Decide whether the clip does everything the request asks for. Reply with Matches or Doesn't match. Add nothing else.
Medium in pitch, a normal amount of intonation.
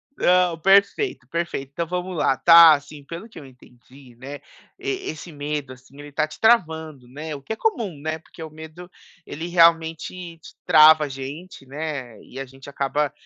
Matches